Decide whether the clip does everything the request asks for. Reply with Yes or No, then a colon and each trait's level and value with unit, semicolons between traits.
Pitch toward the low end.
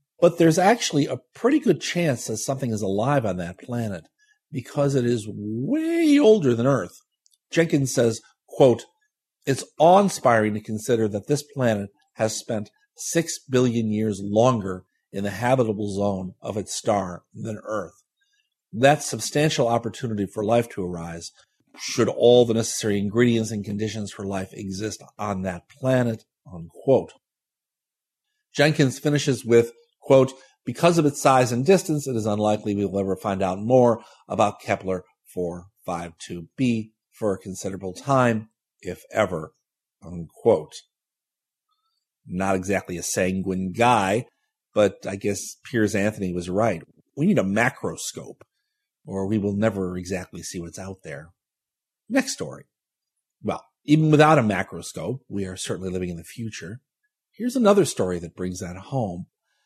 Yes: low, 110 Hz